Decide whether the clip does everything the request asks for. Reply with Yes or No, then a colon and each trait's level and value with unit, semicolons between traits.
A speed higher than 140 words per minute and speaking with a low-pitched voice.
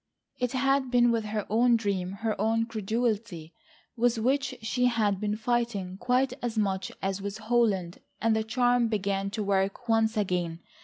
No: average, 165 wpm; high, 220 Hz